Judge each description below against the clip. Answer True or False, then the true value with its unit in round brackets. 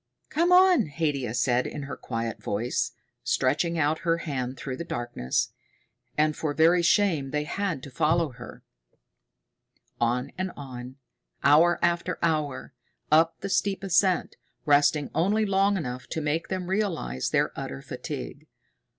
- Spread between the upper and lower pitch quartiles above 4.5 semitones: True (5.2 semitones)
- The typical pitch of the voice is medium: True (155 Hz)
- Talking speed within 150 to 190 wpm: False (140 wpm)